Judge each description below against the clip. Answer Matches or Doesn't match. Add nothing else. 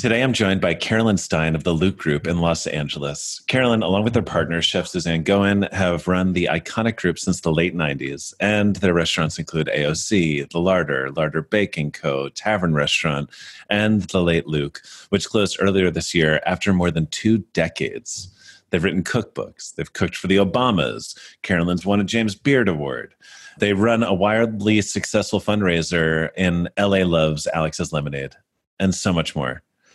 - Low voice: Matches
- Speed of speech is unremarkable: Matches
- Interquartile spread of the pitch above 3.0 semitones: Matches